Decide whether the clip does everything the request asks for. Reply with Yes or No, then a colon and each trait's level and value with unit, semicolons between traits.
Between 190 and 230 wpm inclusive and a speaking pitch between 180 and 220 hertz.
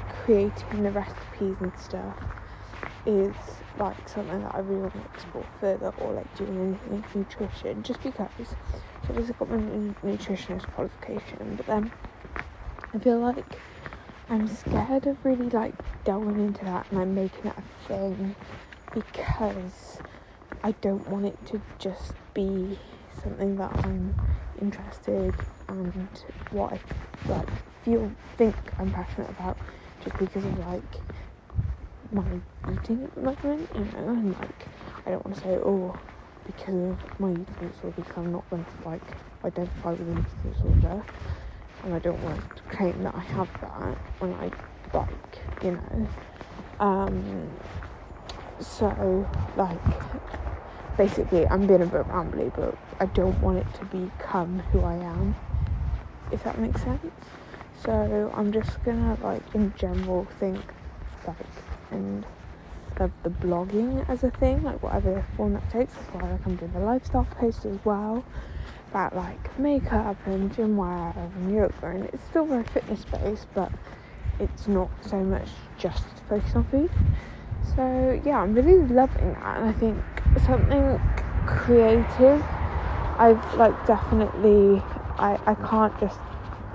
No: average, 150 wpm; high, 190 Hz